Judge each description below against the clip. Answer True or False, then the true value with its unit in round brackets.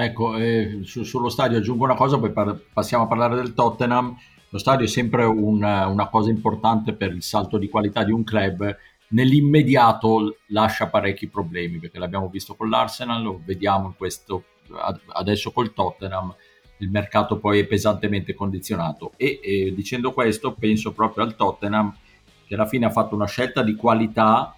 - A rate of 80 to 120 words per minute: False (170 wpm)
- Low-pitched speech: True (110 Hz)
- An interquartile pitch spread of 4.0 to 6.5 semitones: False (2.4 semitones)